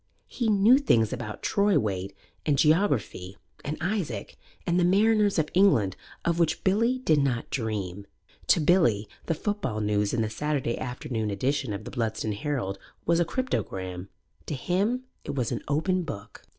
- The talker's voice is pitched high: No, medium, 140 Hz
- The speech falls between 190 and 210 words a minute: No, average, 165 wpm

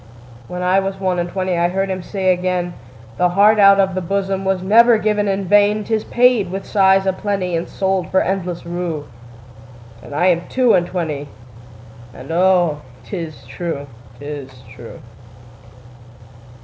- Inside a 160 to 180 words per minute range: No, slow, 135 wpm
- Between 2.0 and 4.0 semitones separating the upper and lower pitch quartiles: No, average, 5.0 semitones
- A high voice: No, medium, 180 Hz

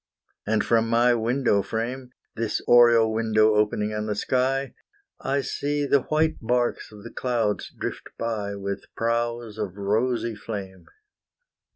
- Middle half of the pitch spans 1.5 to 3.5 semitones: Yes, narrow, 2.6 semitones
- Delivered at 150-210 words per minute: No, average, 140 wpm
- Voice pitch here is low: Yes, low, 115 Hz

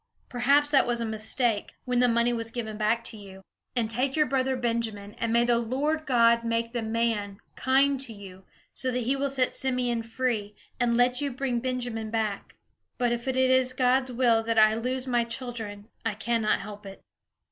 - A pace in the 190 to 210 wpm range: Yes, average, 195 wpm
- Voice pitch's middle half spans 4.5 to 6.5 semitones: No, narrow, 2.4 semitones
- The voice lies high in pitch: Yes, high, 235 Hz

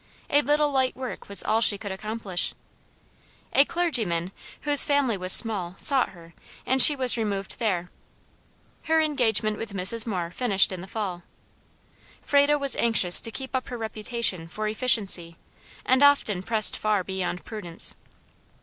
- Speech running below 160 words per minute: Yes, average, 150 wpm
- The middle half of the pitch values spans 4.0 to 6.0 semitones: Yes, wide, 5.5 semitones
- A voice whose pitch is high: Yes, high, 220 Hz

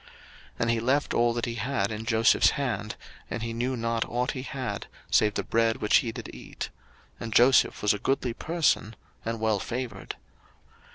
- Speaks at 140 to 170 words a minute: No, average, 185 wpm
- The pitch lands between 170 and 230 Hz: No, low, 115 Hz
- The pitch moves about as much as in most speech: No, narrow, 2.2 semitones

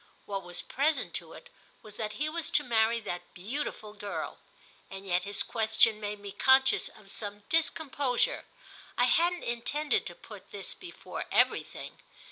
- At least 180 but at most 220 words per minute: No, average, 150 wpm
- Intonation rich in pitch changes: Yes, wide, 6.0 semitones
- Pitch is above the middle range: Yes, high, 225 Hz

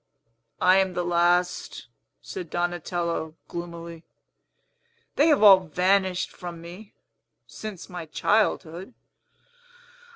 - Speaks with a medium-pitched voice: Yes, medium, 180 Hz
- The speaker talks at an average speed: No, slow, 95 wpm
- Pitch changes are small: Yes, narrow, 2.0 semitones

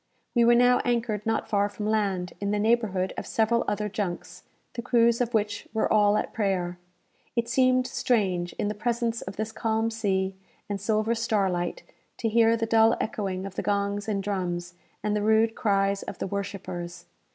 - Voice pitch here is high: Yes, high, 210 Hz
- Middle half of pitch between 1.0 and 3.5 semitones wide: Yes, narrow, 2.6 semitones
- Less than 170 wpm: No, average, 185 wpm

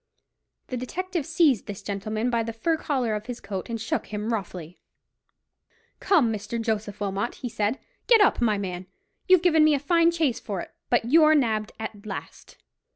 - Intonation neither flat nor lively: No, wide, 6.7 semitones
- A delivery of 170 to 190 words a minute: Yes, average, 180 wpm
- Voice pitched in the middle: No, high, 230 Hz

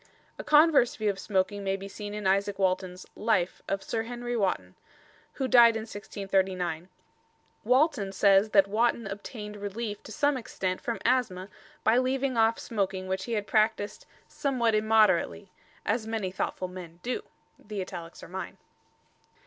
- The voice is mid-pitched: No, high, 205 Hz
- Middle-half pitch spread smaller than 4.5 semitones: Yes, average, 3.3 semitones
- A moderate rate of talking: Yes, average, 155 wpm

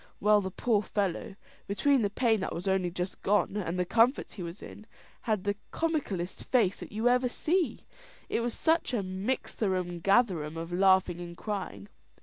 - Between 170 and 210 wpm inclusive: Yes, average, 175 wpm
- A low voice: No, high, 200 Hz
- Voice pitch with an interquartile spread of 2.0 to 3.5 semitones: No, average, 4.3 semitones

